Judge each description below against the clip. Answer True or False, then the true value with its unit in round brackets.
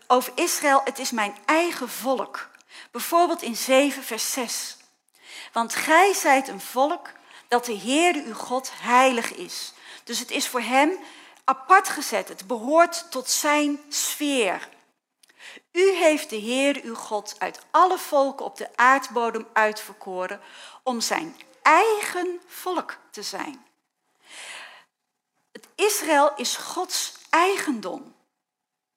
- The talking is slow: True (125 wpm)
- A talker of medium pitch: False (270 Hz)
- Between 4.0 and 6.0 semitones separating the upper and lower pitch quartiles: True (5.3 semitones)